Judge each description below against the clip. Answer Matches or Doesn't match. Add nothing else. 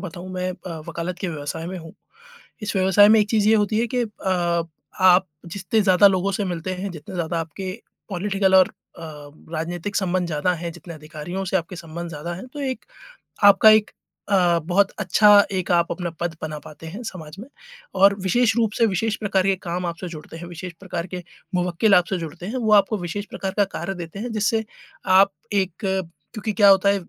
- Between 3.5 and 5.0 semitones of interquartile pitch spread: Doesn't match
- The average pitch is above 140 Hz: Matches